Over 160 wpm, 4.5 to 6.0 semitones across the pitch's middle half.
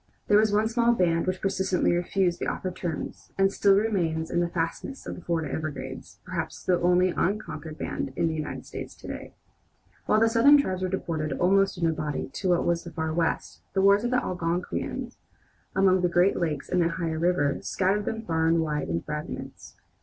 No: fast, 205 wpm; average, 3.2 semitones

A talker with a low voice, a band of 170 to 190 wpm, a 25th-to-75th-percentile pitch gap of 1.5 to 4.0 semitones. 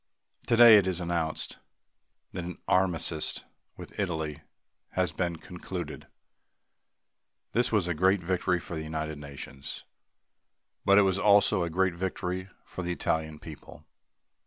No: very low, 90 Hz; slow, 135 wpm; average, 3.0 semitones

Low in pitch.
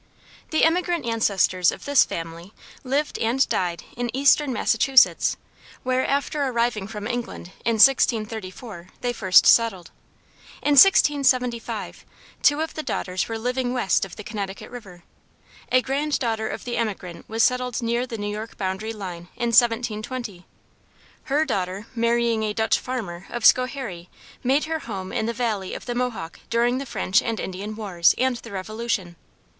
No: high, 230 Hz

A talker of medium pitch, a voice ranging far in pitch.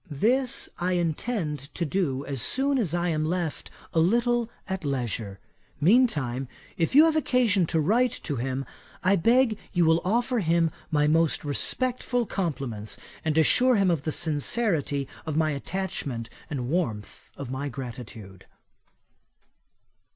Yes: medium, 165 Hz; wide, 7.5 semitones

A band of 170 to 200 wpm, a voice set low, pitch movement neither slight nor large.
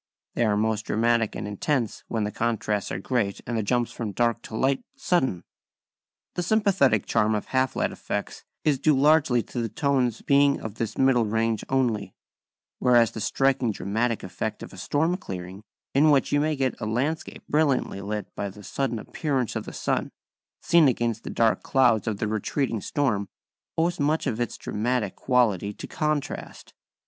Yes: average, 180 wpm; low, 120 Hz; average, 4.4 semitones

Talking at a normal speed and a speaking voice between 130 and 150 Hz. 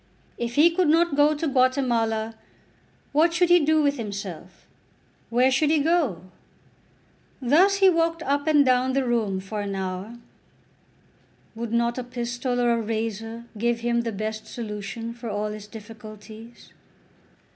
No: average, 150 wpm; high, 235 Hz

